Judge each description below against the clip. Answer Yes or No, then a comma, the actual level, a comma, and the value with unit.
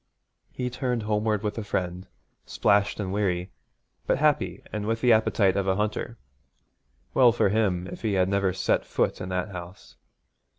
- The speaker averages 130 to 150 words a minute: No, average, 170 wpm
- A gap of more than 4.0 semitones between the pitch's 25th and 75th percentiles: No, average, 3.1 semitones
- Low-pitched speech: Yes, low, 105 Hz